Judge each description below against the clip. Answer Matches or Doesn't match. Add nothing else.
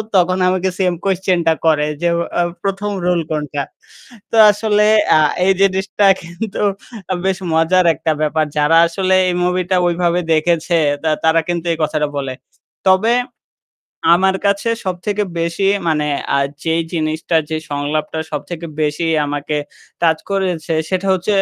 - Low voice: Doesn't match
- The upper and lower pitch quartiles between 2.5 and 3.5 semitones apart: Matches